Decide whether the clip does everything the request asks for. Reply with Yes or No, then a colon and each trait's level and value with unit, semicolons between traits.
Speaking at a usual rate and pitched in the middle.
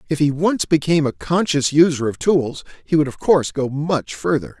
No: fast, 210 wpm; medium, 145 Hz